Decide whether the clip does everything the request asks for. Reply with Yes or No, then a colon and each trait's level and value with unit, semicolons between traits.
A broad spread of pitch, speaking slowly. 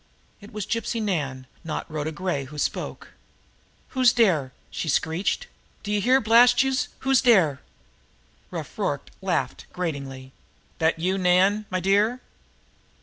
Yes: wide, 6.6 semitones; slow, 130 wpm